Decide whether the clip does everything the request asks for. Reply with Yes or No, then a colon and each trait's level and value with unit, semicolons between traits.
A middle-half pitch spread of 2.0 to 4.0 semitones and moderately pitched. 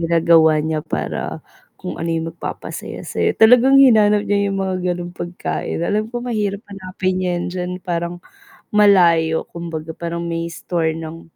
Yes: average, 3.3 semitones; medium, 175 Hz